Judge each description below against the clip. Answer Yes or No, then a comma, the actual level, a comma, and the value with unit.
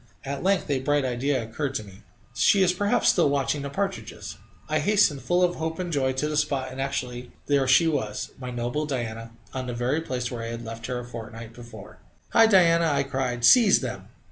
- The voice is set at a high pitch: No, low, 135 Hz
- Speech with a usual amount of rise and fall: Yes, average, 4.9 semitones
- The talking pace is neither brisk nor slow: No, fast, 215 wpm